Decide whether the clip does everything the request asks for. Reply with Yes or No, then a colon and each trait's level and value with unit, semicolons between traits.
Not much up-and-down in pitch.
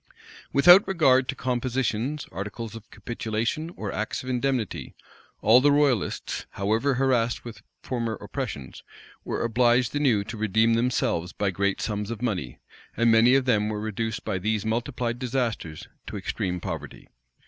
No: average, 3.3 semitones